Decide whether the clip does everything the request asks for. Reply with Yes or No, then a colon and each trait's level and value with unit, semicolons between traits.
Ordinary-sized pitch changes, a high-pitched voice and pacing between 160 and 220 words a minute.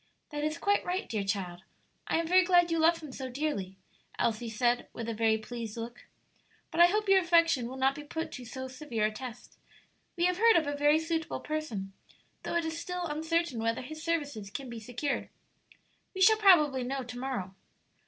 No: wide, 6.1 semitones; very high, 285 Hz; fast, 205 wpm